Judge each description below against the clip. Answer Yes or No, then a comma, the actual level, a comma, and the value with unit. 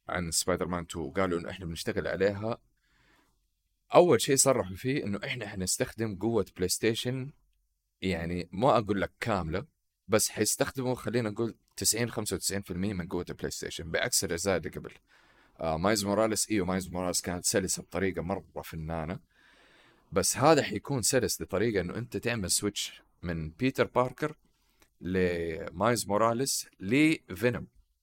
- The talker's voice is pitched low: Yes, low, 100 Hz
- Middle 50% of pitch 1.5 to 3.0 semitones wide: No, average, 5.1 semitones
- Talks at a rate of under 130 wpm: No, fast, 135 wpm